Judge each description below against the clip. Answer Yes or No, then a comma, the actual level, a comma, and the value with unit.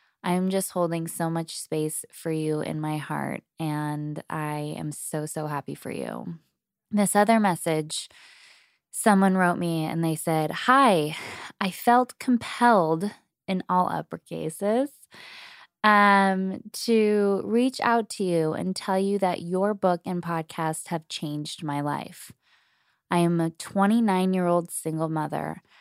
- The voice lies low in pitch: No, medium, 180 Hz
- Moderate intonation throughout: Yes, average, 4.4 semitones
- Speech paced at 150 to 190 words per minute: No, slow, 135 wpm